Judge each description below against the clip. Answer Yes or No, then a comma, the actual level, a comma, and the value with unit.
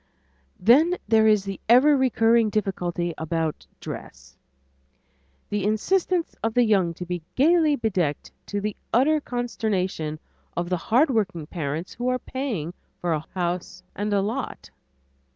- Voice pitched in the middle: No, high, 210 Hz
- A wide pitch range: Yes, wide, 5.9 semitones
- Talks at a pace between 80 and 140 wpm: Yes, slow, 135 wpm